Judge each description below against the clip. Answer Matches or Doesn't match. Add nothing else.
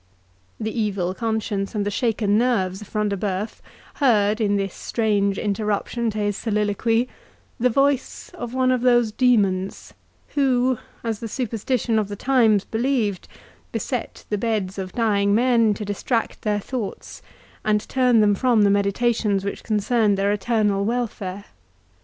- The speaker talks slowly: Doesn't match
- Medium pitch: Doesn't match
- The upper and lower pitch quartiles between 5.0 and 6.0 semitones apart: Doesn't match